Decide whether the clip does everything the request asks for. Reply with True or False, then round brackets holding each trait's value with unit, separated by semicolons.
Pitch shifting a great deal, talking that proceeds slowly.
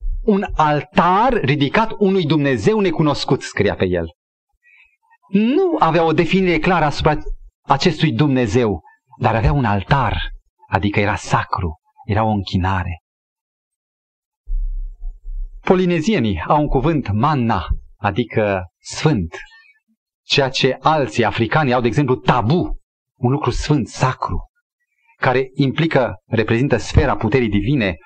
True (8.1 semitones; 110 wpm)